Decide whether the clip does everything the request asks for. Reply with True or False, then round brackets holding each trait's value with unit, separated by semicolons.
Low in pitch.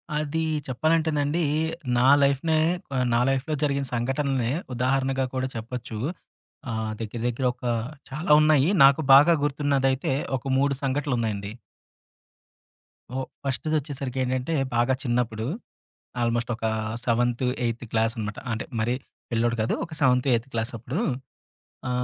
True (130 Hz)